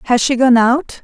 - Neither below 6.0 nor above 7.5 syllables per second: No, 4.7 syllables/s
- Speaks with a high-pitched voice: Yes, very high, 250 Hz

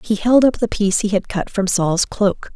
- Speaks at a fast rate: Yes, fast, 260 wpm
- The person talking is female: Yes, female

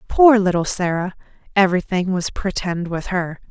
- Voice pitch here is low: No, medium, 185 Hz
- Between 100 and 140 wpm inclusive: Yes, slow, 135 wpm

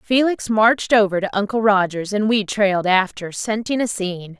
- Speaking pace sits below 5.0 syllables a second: No, 5.1 syllables/s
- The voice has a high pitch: Yes, high, 210 Hz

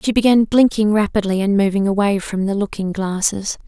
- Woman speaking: Yes, female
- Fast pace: No, average, 180 wpm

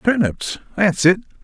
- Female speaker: No, male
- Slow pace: Yes, slow, 125 wpm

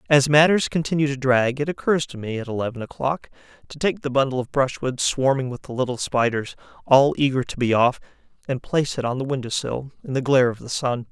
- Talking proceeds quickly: Yes, fast, 220 wpm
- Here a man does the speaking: Yes, male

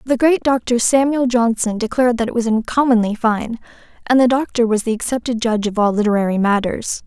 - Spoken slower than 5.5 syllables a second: No, 5.8 syllables/s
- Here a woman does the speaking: Yes, female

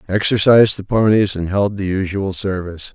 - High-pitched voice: No, low, 100 Hz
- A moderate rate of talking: Yes, average, 165 wpm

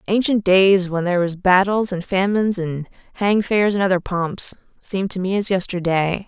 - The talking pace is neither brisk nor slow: Yes, average, 180 wpm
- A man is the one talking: No, female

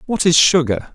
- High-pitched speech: No, medium, 160 Hz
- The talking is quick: No, average, 190 wpm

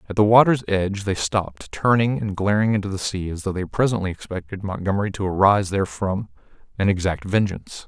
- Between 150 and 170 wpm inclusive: No, average, 185 wpm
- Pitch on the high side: No, low, 100 Hz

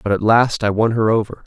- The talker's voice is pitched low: Yes, low, 110 Hz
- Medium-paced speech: No, fast, 285 wpm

